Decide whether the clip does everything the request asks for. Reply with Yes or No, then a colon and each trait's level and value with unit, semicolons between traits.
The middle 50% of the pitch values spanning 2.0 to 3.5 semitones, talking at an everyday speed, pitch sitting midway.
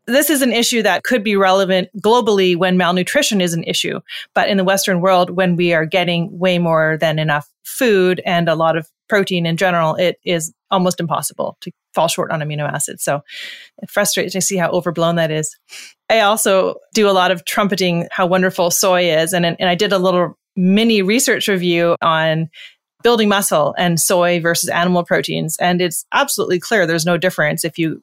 Yes: average, 2.7 semitones; average, 195 wpm; medium, 180 Hz